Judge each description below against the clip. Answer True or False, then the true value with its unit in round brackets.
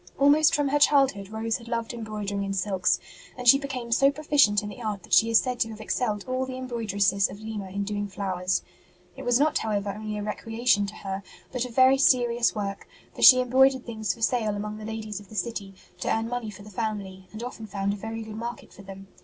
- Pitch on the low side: False (220 Hz)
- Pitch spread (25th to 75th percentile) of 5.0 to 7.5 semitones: False (3.3 semitones)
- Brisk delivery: True (235 wpm)